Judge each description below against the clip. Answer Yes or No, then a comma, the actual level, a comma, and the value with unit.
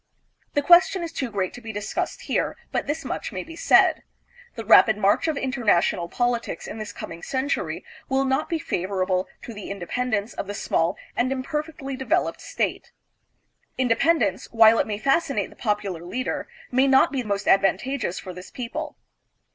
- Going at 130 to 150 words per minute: No, average, 175 wpm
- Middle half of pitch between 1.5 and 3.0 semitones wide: No, average, 5.2 semitones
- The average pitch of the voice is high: Yes, high, 240 Hz